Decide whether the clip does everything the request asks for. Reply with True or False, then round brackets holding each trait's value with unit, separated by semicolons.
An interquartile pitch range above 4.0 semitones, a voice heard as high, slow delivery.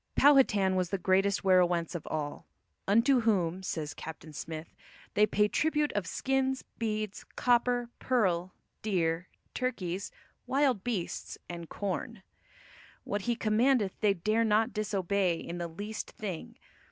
True (4.6 semitones; 200 Hz; 130 wpm)